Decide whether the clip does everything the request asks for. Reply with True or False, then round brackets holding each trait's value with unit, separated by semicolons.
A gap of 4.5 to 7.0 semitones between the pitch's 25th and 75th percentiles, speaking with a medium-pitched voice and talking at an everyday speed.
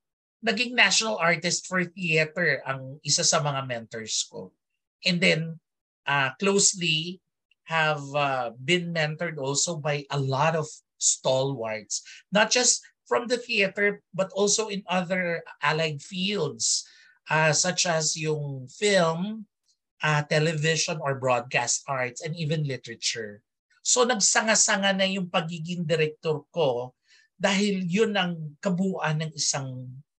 True (4.8 semitones; 165 Hz; 125 wpm)